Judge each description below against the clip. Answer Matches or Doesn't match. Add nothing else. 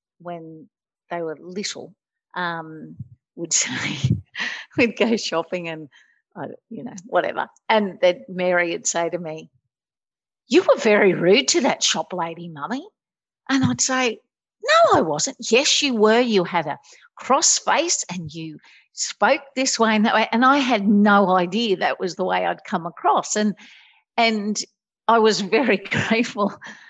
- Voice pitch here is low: Doesn't match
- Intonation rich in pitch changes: Matches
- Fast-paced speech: Doesn't match